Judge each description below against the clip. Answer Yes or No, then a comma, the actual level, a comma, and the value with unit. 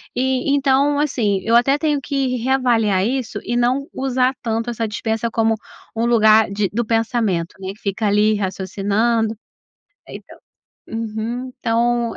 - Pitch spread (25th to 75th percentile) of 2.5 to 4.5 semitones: Yes, average, 2.9 semitones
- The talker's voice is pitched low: No, high, 230 Hz